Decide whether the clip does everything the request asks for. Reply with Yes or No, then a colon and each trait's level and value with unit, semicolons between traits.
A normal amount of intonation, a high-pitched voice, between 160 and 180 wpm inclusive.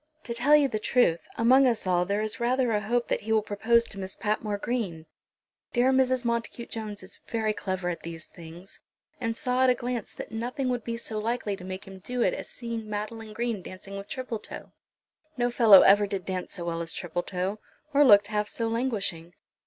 No: average, 3.7 semitones; high, 215 Hz; fast, 205 wpm